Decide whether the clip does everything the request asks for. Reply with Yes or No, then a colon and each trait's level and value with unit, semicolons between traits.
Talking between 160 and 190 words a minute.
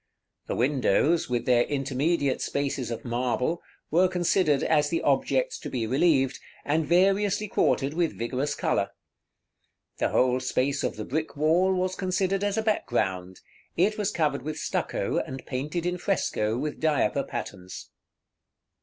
No: average, 145 wpm